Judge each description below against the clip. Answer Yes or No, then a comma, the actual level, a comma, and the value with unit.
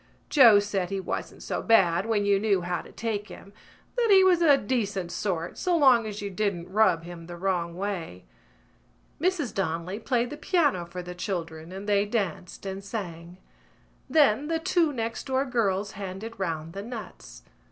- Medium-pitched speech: No, high, 200 Hz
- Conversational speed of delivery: Yes, average, 175 wpm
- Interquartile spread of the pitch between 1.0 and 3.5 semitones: No, average, 4.8 semitones